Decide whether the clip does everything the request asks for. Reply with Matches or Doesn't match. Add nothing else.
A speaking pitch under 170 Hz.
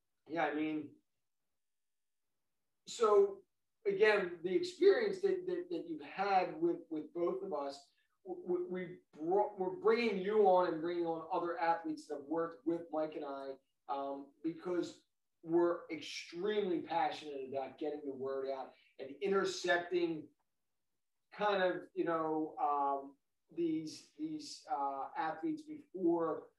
Doesn't match